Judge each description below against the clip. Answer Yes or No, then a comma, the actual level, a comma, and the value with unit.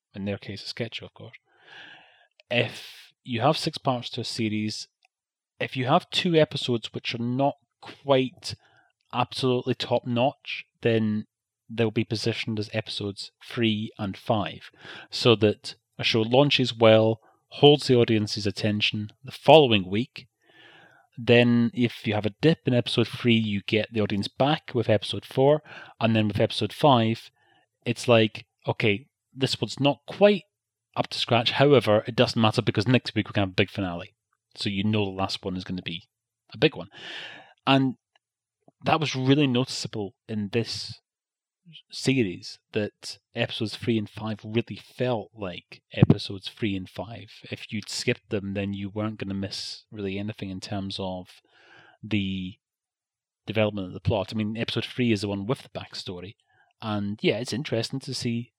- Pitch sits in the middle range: No, low, 115 Hz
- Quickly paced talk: No, average, 170 wpm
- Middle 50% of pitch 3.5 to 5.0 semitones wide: No, average, 3.0 semitones